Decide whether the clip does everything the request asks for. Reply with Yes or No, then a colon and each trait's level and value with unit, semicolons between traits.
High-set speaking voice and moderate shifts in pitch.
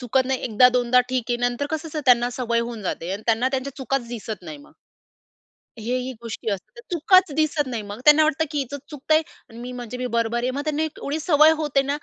Yes: very high, 255 Hz; average, 3.8 semitones